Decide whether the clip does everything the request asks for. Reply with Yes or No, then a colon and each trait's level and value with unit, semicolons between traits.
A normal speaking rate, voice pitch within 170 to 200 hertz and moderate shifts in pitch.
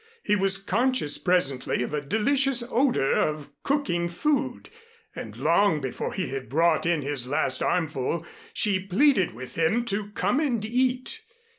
No: average, 150 wpm; high, 190 Hz; wide, 8.2 semitones